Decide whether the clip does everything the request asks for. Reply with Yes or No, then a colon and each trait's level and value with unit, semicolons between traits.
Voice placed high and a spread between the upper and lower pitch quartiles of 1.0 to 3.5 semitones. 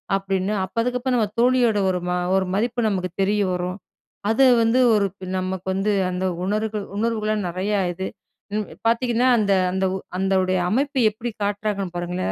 Yes: high, 205 Hz; average, 3.2 semitones